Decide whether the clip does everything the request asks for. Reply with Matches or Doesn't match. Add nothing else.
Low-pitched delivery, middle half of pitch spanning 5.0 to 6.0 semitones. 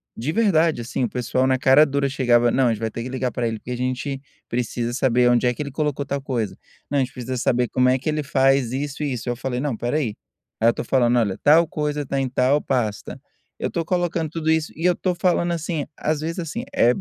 Doesn't match